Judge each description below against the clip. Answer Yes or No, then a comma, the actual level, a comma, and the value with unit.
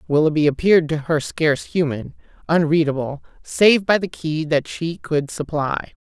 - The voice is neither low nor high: Yes, medium, 155 Hz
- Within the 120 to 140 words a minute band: No, average, 150 wpm